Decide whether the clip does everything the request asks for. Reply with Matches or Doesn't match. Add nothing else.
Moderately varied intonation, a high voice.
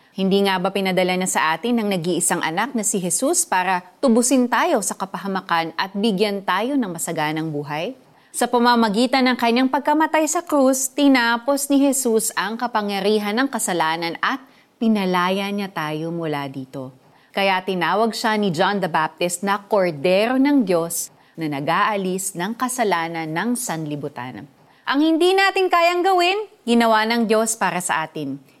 Doesn't match